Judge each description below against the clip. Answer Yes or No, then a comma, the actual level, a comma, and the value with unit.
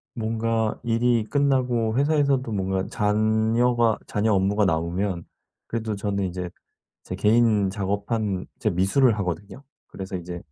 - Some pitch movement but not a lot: Yes, average, 3.2 semitones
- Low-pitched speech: Yes, low, 105 Hz